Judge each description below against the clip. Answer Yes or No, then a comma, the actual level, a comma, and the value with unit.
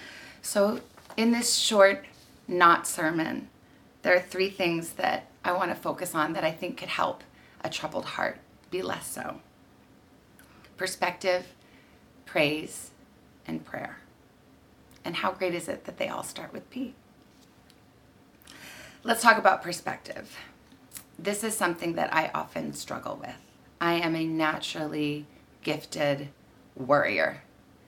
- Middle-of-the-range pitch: Yes, medium, 180 Hz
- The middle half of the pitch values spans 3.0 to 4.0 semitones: No, average, 4.6 semitones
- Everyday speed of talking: No, slow, 130 wpm